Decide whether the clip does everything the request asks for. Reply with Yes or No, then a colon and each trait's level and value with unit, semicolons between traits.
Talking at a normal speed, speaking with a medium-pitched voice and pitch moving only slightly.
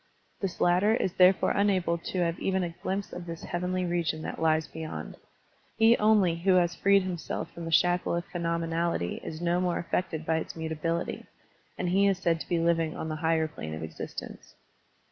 Yes: average, 195 wpm; medium, 170 Hz; narrow, 2.0 semitones